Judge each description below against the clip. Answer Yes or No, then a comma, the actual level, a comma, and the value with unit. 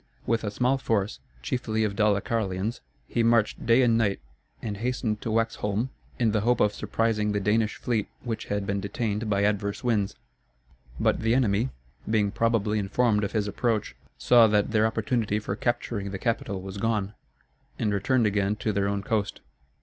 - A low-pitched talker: Yes, low, 105 Hz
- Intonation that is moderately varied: No, narrow, 2.2 semitones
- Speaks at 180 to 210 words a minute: No, average, 170 wpm